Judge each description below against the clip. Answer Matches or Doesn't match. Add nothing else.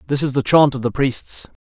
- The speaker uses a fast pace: Matches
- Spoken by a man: Matches